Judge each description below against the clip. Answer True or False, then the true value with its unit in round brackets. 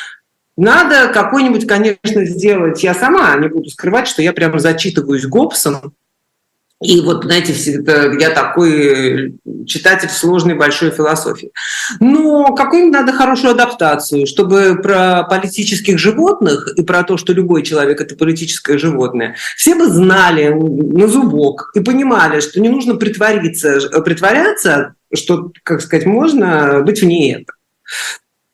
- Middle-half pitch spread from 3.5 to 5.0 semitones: False (5.4 semitones)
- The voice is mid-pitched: True (175 Hz)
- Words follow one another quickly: False (130 wpm)